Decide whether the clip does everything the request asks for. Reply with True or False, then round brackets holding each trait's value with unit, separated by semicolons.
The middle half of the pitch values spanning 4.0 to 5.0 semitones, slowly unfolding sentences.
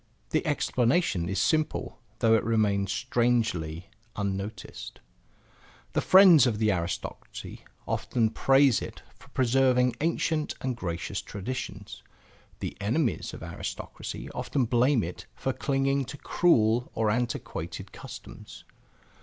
True (4.6 semitones; 110 wpm)